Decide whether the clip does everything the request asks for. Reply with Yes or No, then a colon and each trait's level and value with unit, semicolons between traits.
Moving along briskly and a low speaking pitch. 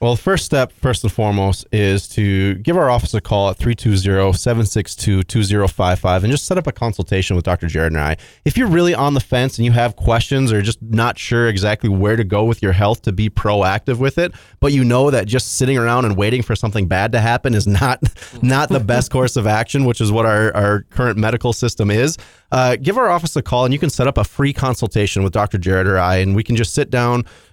Yes: fast, 235 wpm; low, 115 Hz